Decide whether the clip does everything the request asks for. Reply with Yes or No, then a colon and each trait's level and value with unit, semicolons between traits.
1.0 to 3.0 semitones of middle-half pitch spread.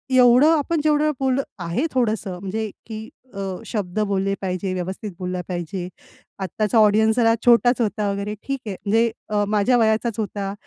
No: average, 3.5 semitones